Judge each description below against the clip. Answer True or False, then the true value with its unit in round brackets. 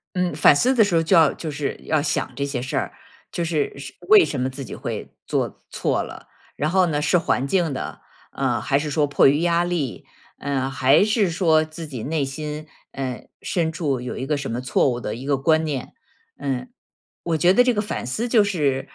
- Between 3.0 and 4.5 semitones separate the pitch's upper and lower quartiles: True (4.0 semitones)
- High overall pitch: False (150 Hz)